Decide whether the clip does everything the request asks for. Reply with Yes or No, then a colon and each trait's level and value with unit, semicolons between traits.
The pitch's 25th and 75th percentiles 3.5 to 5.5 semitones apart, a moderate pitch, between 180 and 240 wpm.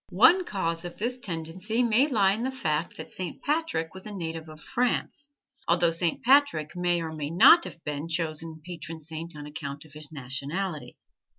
Yes: average, 5.2 semitones; medium, 170 Hz; average, 185 wpm